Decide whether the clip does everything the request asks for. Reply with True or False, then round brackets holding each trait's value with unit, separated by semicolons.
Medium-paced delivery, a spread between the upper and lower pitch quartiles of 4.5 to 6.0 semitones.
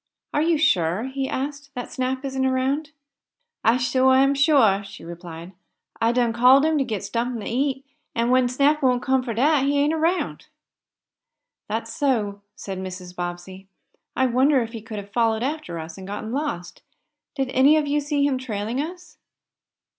True (175 wpm; 4.9 semitones)